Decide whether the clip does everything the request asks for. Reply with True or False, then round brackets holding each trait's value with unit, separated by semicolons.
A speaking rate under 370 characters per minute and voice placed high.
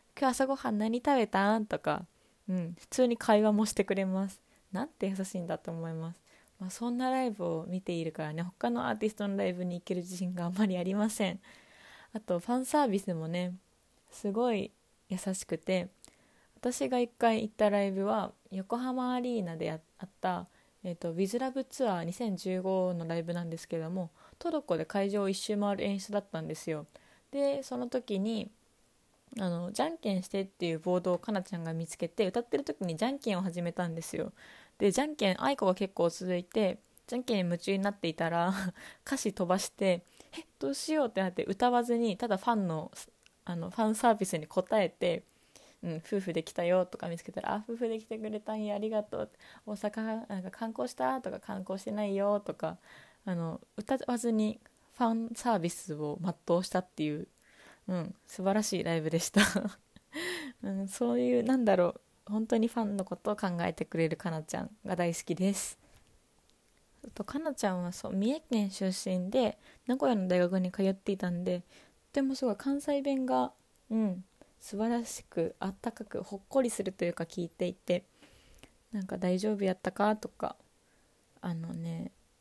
True (355 characters per minute; 195 Hz)